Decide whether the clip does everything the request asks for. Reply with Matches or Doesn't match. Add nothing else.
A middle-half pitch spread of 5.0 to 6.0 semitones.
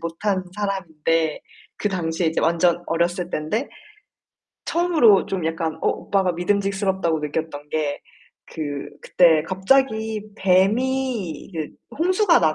Doesn't match